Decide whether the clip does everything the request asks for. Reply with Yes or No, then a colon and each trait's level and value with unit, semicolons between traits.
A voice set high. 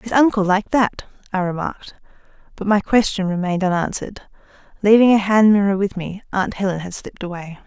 Yes: high, 200 Hz